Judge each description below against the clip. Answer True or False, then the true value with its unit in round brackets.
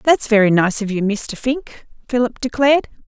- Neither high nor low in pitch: False (235 Hz)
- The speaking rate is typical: True (175 wpm)